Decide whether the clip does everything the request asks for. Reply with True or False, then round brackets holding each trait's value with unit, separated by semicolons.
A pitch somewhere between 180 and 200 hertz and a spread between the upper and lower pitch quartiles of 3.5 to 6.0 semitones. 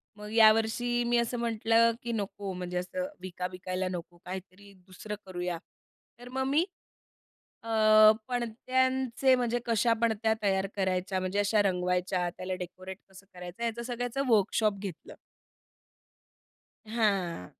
False (210 Hz; 4.1 semitones)